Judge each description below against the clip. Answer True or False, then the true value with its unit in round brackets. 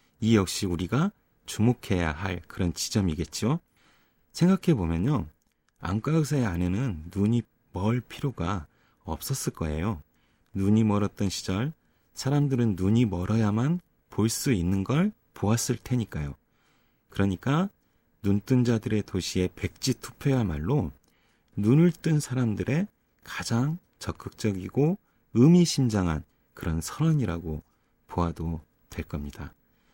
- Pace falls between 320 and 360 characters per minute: False (250 characters per minute)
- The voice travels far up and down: True (6.5 semitones)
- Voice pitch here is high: False (110 Hz)